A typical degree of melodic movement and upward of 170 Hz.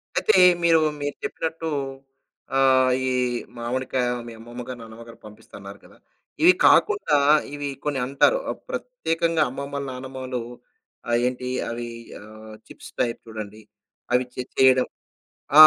No: average, 3.5 semitones; low, 130 Hz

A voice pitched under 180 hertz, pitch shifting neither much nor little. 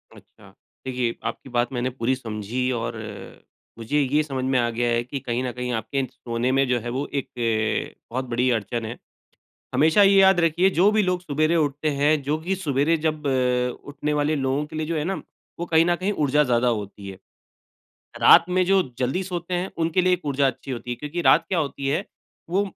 Yes: medium, 140 Hz; average, 4.9 semitones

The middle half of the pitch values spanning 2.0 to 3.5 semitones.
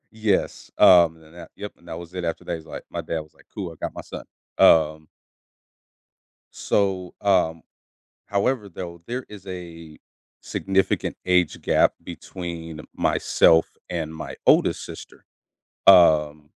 Yes: average, 2.8 semitones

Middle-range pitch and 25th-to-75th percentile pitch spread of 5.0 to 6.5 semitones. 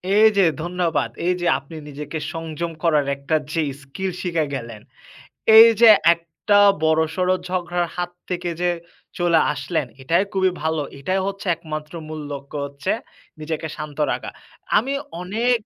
No: medium, 165 Hz; average, 3.0 semitones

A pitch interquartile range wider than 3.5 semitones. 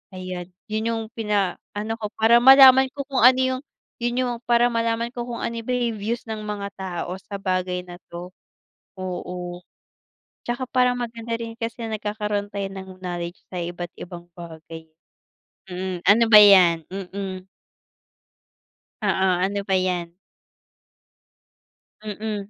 Yes: average, 4.0 semitones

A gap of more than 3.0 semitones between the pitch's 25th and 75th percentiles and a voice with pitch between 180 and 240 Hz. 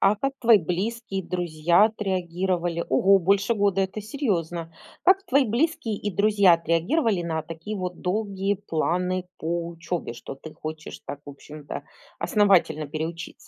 Yes: average, 3.9 semitones; medium, 185 Hz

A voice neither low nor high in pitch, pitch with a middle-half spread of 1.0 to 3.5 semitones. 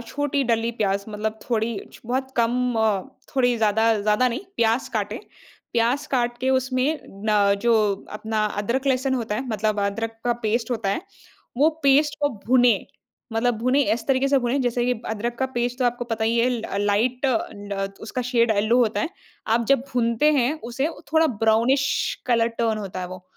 No: high, 235 Hz; average, 2.7 semitones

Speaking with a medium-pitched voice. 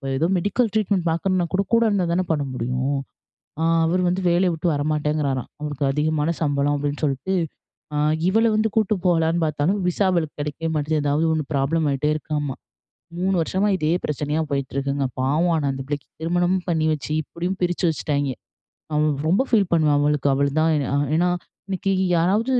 Yes: medium, 155 Hz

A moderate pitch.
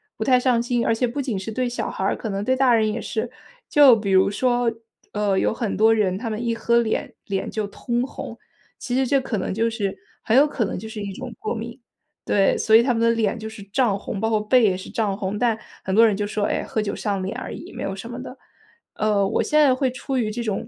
No: high, 225 Hz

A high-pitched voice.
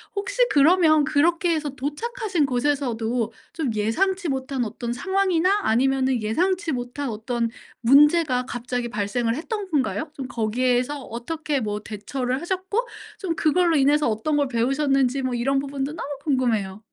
Yes: very high, 275 Hz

